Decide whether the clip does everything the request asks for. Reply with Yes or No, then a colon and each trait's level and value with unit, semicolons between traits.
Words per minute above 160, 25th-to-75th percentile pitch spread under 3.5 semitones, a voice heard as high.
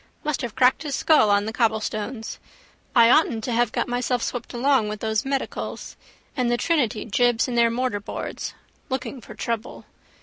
Yes: average, 170 wpm; average, 2.7 semitones; high, 240 Hz